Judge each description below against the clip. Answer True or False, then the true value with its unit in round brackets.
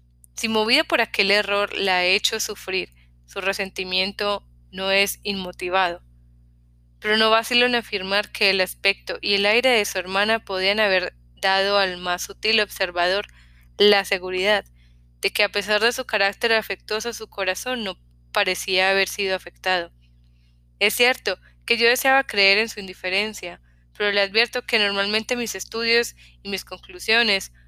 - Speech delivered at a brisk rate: False (155 wpm)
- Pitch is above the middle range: True (195 Hz)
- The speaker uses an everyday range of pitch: True (3.0 semitones)